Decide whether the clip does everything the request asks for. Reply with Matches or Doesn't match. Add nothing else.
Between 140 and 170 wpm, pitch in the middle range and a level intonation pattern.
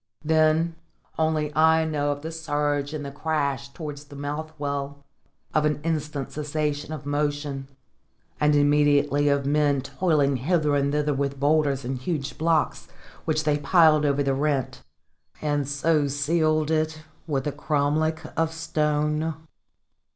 Matches